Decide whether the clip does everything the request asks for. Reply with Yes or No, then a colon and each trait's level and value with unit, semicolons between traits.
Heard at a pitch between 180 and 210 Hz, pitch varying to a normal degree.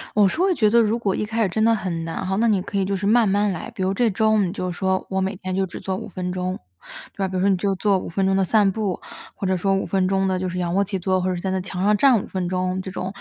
No: high, 190 Hz; narrow, 1.9 semitones